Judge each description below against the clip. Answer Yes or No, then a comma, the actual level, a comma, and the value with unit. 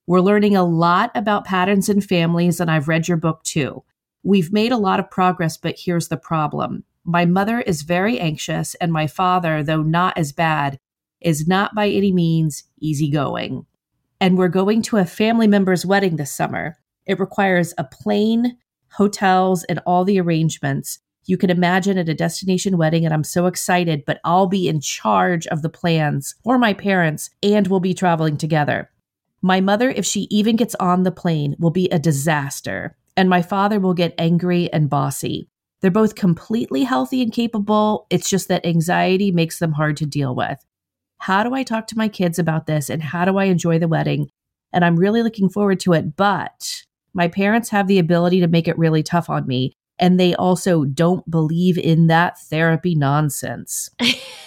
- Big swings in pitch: No, average, 3.5 semitones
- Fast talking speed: No, average, 185 wpm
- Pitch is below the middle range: No, medium, 175 Hz